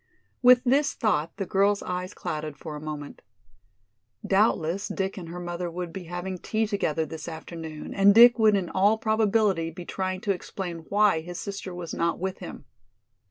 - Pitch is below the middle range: No, medium, 185 Hz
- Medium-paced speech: Yes, average, 175 wpm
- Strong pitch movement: No, average, 3.5 semitones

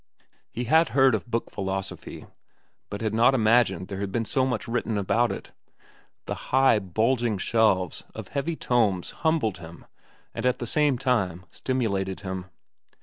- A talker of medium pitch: No, low, 115 Hz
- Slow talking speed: No, average, 155 wpm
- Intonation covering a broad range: No, average, 4.6 semitones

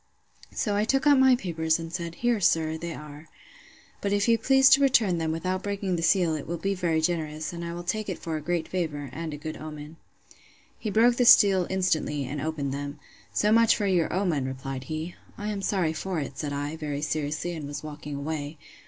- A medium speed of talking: No, fast, 220 wpm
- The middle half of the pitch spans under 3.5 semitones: No, average, 4.4 semitones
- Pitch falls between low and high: Yes, medium, 165 Hz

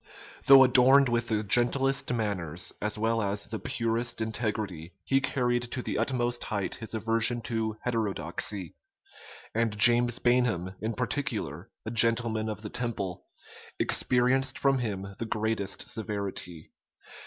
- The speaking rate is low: Yes, slow, 130 wpm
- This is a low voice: Yes, low, 115 Hz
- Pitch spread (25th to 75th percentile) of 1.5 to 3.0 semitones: Yes, average, 2.7 semitones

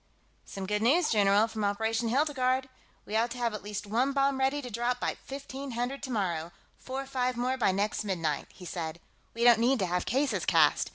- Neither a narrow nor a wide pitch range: Yes, average, 4.4 semitones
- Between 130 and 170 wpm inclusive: No, fast, 205 wpm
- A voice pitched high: Yes, high, 235 Hz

